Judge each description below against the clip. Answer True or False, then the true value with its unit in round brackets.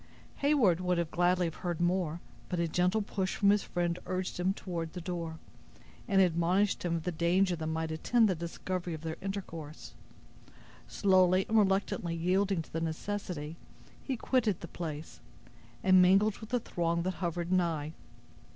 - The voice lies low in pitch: False (180 Hz)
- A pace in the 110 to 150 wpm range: False (165 wpm)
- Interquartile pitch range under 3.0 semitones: True (2.5 semitones)